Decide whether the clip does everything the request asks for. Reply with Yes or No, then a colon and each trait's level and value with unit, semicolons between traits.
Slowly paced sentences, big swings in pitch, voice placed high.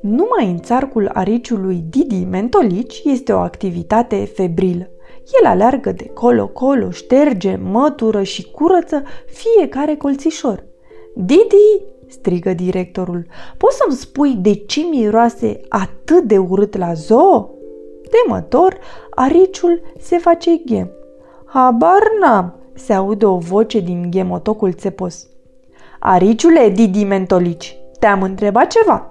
Yes: slow, 110 wpm; wide, 8.9 semitones; high, 225 Hz